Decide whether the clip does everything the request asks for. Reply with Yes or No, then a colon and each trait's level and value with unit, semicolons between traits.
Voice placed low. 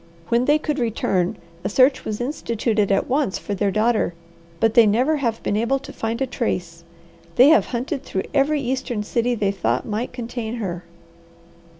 No: high, 235 Hz